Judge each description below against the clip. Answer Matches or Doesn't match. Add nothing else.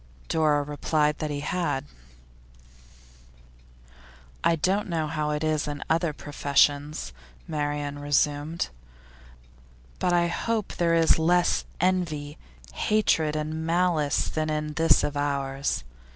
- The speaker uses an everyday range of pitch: Doesn't match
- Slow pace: Matches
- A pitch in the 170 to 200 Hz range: Doesn't match